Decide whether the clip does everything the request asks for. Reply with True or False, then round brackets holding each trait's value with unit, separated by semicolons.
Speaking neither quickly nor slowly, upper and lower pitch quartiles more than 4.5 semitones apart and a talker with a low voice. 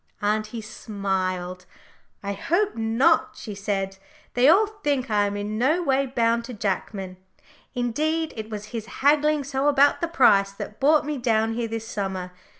False (160 wpm; 5.6 semitones; 225 Hz)